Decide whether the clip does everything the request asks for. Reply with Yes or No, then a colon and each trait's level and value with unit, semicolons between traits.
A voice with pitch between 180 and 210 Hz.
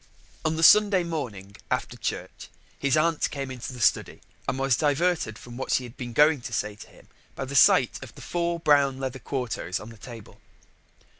No: low, 135 Hz